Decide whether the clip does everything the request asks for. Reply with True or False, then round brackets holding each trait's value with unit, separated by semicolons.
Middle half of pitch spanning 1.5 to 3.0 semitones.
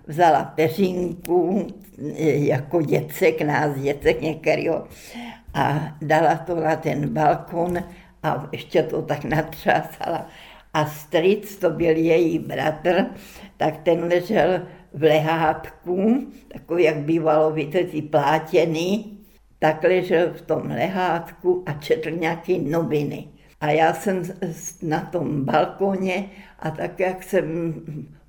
True (2.7 semitones)